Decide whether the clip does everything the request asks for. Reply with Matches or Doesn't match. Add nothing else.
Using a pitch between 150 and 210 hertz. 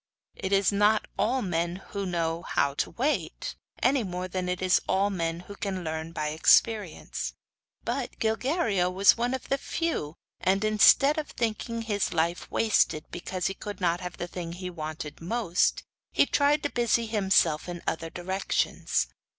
Matches